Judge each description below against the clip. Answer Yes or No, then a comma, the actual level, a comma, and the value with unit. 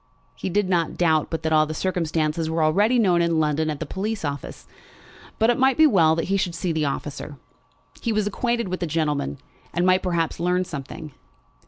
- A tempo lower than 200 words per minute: No, fast, 205 wpm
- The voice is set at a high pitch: No, medium, 170 Hz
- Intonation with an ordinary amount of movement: Yes, average, 3.4 semitones